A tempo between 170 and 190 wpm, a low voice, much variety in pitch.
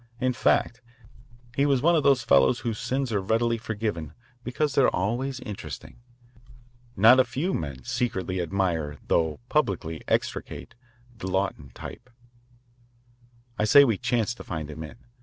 No: average, 150 wpm; low, 110 Hz; wide, 7.0 semitones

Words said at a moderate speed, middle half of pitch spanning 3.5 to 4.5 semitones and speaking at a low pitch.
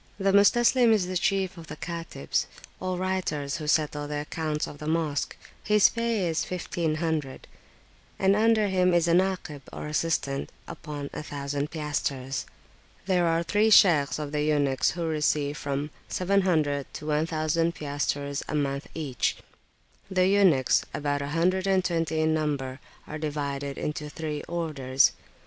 No: average, 150 wpm; average, 3.9 semitones; medium, 155 Hz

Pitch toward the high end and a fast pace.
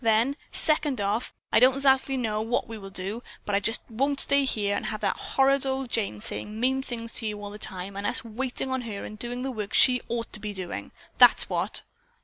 Yes: high, 230 Hz; fast, 230 wpm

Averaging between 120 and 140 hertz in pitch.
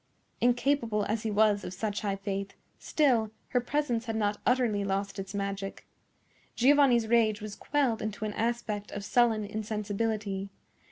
No: high, 215 Hz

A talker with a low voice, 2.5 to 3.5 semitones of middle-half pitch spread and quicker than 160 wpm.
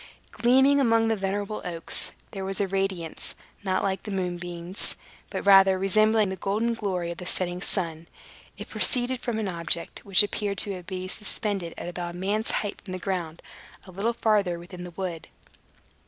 No: high, 195 Hz; average, 2.8 semitones; average, 175 wpm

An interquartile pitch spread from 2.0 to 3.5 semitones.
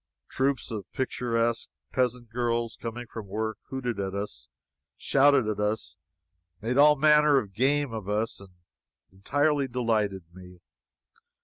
No: average, 4.1 semitones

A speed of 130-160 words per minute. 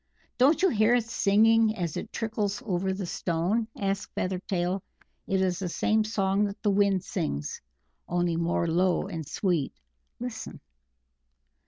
Yes: average, 145 wpm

